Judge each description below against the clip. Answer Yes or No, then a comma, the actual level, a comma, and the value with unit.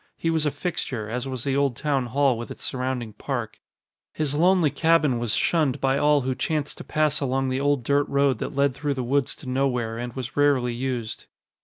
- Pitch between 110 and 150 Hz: Yes, low, 135 Hz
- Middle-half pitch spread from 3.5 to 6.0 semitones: No, average, 2.7 semitones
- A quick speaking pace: Yes, fast, 210 wpm